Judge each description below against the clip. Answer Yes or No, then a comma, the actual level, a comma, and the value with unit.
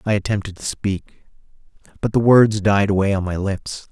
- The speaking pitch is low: Yes, low, 100 Hz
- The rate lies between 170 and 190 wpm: Yes, average, 185 wpm